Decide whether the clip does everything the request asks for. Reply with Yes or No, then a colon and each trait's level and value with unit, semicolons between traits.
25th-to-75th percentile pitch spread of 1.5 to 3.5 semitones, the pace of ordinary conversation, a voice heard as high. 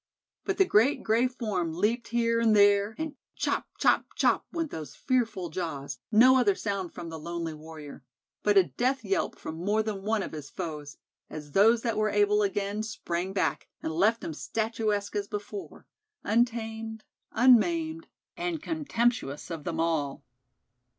No: wide, 5.5 semitones; average, 160 wpm; high, 210 Hz